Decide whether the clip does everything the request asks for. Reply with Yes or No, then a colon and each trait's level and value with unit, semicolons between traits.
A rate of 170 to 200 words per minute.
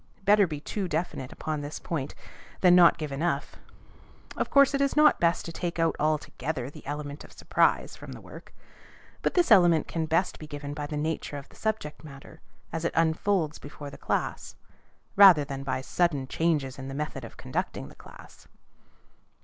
Yes: average, 190 wpm